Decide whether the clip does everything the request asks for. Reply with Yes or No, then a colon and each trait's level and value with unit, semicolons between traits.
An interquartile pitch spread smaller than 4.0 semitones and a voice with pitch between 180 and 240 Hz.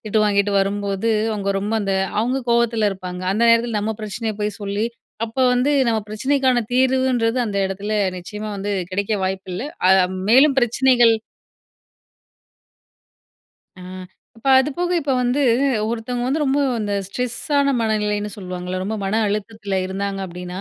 Yes: average, 3.6 semitones; high, 215 Hz